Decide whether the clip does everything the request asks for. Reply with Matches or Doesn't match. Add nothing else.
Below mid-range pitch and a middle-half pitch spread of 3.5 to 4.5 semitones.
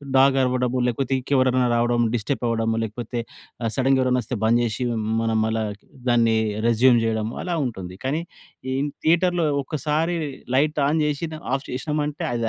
Matches